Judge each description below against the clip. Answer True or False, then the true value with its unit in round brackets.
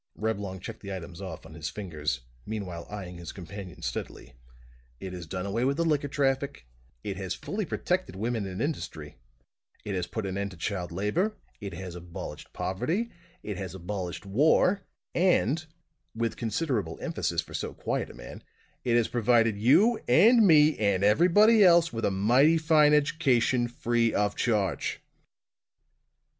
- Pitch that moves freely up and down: True (7.3 semitones)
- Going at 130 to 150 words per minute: False (160 wpm)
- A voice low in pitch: True (105 Hz)